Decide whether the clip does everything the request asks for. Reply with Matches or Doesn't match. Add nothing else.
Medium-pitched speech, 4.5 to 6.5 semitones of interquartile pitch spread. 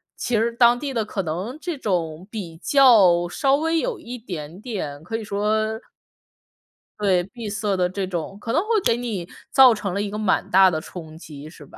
Doesn't match